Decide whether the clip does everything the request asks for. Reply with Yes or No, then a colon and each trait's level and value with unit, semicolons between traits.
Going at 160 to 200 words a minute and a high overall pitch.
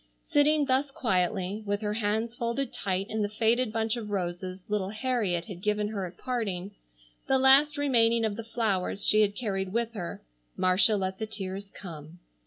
Yes: average, 180 wpm; high, 210 Hz